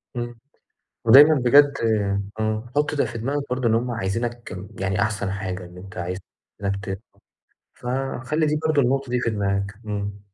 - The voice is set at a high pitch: No, low, 115 Hz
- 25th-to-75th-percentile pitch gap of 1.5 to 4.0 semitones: No, average, 4.9 semitones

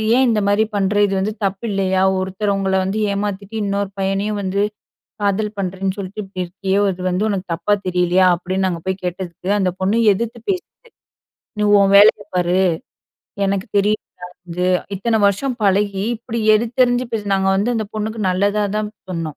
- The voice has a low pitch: No, high, 195 Hz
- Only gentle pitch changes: Yes, narrow, 2.1 semitones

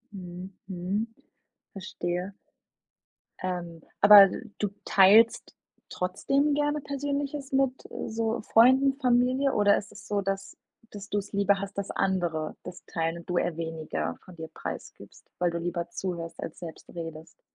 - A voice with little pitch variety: No, average, 4.7 semitones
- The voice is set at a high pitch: Yes, high, 195 Hz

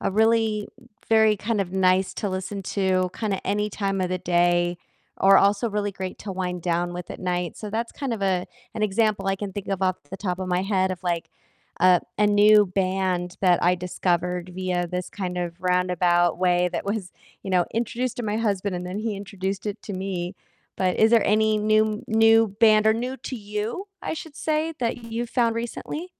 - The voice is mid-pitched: No, high, 195 Hz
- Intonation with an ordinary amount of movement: Yes, average, 3.1 semitones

